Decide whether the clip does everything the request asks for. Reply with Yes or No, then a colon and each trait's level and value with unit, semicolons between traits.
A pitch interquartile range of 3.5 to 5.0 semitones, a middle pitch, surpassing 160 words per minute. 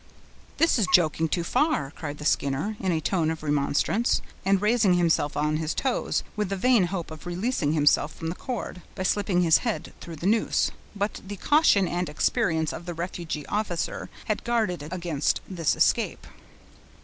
Yes: average, 4.6 semitones; medium, 175 Hz; average, 175 wpm